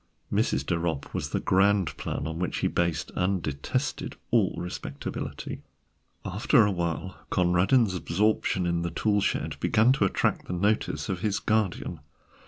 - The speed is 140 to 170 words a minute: Yes, average, 155 wpm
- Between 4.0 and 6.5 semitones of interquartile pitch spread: No, average, 3.1 semitones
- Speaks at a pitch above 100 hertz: No, very low, 90 Hz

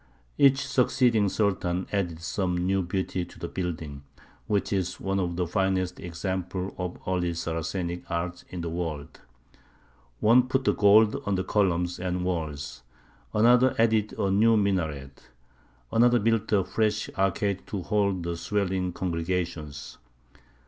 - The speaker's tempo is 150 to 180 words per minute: No, average, 140 wpm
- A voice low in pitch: Yes, very low, 95 Hz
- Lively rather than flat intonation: No, average, 3.1 semitones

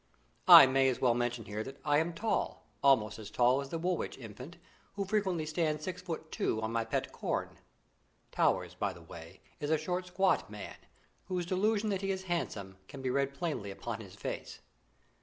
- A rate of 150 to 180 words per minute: No, average, 195 wpm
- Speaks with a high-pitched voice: No, medium, 150 Hz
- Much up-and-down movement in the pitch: Yes, wide, 6.9 semitones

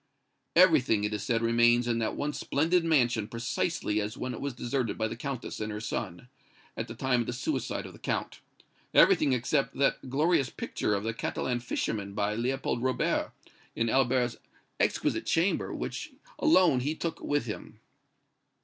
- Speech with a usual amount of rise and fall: Yes, average, 3.5 semitones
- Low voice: Yes, low, 125 Hz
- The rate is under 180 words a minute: Yes, average, 170 wpm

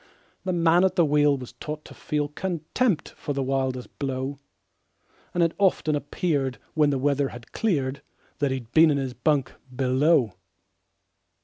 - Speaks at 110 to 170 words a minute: Yes, average, 155 wpm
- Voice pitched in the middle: Yes, medium, 145 Hz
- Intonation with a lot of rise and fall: No, average, 3.5 semitones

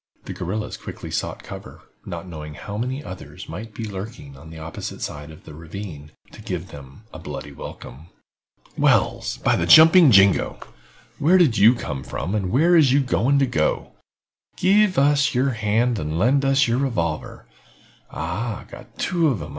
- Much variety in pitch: Yes, wide, 9.0 semitones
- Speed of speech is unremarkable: Yes, average, 170 wpm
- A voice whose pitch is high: No, low, 105 Hz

